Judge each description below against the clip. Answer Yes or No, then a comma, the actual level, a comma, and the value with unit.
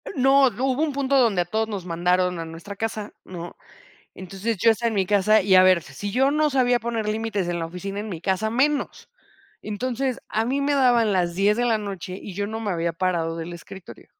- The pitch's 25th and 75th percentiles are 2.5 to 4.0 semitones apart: No, average, 4.7 semitones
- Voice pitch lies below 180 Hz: No, high, 205 Hz